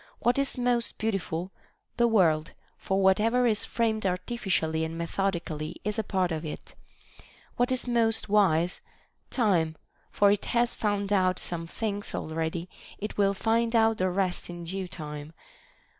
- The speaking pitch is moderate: No, high, 195 Hz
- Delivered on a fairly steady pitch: No, average, 4.8 semitones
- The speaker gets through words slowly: No, average, 160 wpm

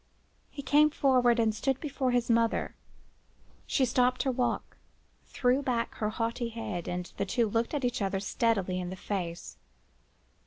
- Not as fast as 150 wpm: No, average, 155 wpm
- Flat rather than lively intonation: No, average, 3.7 semitones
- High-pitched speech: Yes, high, 235 Hz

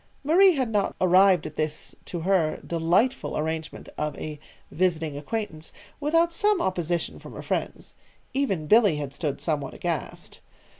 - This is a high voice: No, medium, 175 Hz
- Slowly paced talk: No, average, 145 wpm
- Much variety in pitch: Yes, wide, 6.6 semitones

